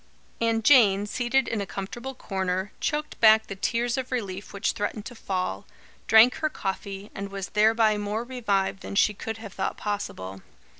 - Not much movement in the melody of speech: No, average, 3.1 semitones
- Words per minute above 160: Yes, average, 170 wpm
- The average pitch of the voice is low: No, high, 210 Hz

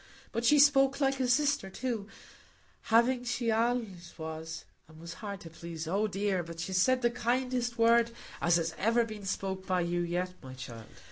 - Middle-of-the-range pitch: No, high, 205 Hz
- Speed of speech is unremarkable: Yes, average, 165 wpm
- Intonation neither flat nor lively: No, wide, 5.9 semitones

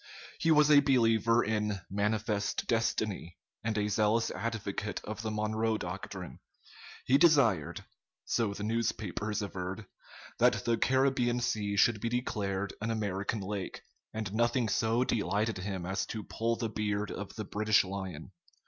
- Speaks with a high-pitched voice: No, low, 110 Hz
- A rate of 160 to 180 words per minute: No, average, 145 wpm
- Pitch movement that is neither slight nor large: No, narrow, 2.3 semitones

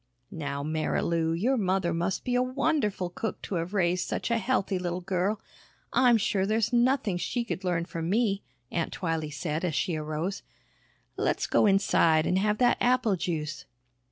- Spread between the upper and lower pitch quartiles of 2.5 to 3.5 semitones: No, average, 4.9 semitones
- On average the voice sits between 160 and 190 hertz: Yes, medium, 185 Hz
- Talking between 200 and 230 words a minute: No, average, 170 wpm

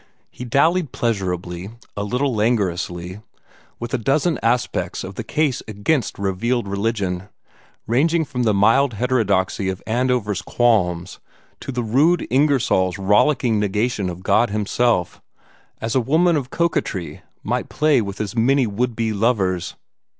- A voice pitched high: No, low, 115 Hz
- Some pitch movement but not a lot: Yes, average, 4.6 semitones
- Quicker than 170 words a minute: No, slow, 135 wpm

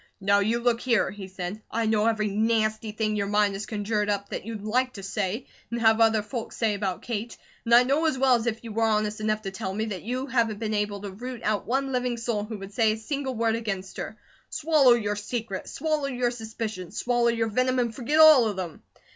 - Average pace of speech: No, fast, 235 wpm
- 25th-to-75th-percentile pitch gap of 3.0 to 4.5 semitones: No, narrow, 2.6 semitones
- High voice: Yes, high, 220 Hz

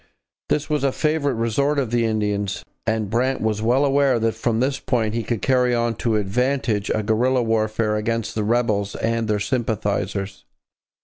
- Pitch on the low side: Yes, low, 115 Hz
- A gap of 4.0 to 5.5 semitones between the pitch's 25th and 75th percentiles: No, average, 3.1 semitones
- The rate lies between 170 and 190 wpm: Yes, average, 175 wpm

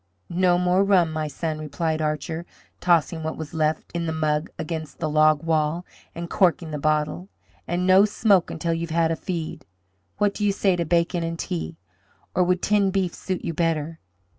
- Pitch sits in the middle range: Yes, medium, 165 Hz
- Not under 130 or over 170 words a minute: No, average, 190 wpm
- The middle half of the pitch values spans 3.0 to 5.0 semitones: No, narrow, 2.4 semitones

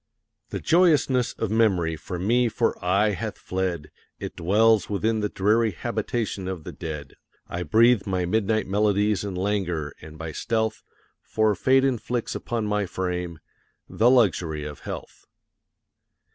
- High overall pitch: No, low, 105 Hz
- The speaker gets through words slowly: No, average, 145 wpm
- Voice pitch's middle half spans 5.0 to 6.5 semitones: No, average, 4.1 semitones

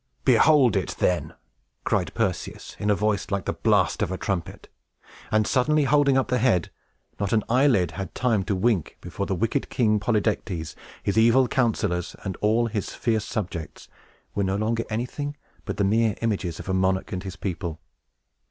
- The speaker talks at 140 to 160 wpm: No, average, 175 wpm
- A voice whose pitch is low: Yes, low, 105 Hz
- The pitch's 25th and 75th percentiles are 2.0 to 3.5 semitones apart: No, average, 3.9 semitones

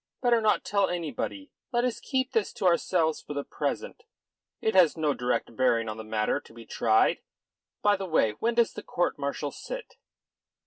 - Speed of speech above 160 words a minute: Yes, average, 185 wpm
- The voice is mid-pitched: Yes, medium, 180 Hz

